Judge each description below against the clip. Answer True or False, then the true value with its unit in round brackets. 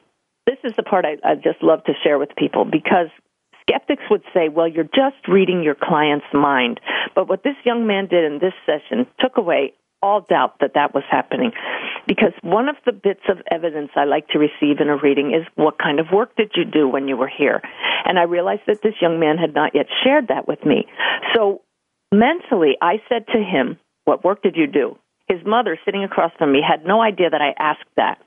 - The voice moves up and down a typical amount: False (6.3 semitones)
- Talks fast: True (220 wpm)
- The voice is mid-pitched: True (175 Hz)